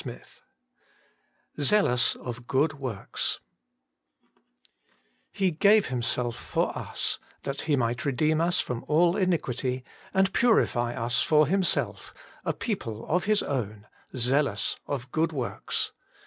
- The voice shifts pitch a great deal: Yes, wide, 6.2 semitones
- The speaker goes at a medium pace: No, slow, 120 wpm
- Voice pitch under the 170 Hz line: Yes, medium, 140 Hz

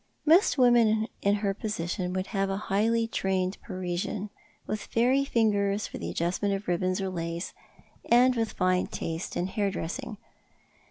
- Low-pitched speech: No, high, 200 Hz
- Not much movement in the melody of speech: No, average, 3.5 semitones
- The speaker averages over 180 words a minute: No, average, 155 wpm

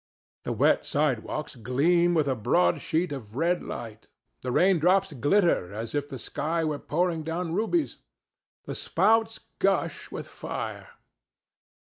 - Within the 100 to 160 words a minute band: Yes, slow, 135 wpm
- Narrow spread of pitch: No, wide, 5.6 semitones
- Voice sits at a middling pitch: Yes, medium, 155 Hz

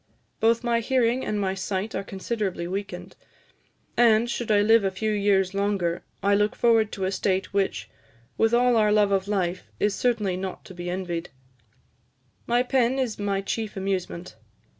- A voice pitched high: Yes, high, 205 Hz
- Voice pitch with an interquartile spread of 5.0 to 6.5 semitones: No, average, 3.0 semitones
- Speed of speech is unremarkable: Yes, average, 170 wpm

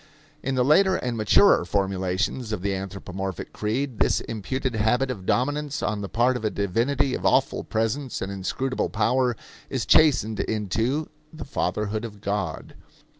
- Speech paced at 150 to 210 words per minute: Yes, average, 155 wpm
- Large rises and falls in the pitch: No, average, 4.6 semitones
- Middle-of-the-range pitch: No, low, 110 Hz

